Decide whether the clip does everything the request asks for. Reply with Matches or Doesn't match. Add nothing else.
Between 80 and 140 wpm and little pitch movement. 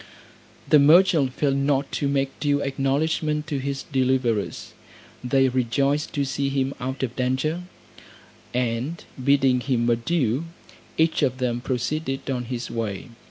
Matches